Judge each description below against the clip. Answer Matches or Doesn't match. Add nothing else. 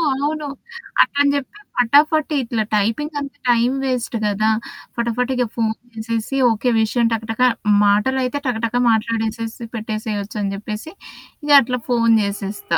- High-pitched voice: Matches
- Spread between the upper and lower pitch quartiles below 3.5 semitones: Matches